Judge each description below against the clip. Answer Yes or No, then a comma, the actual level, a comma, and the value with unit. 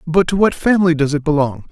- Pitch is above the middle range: No, medium, 160 Hz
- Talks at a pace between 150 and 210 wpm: No, fast, 245 wpm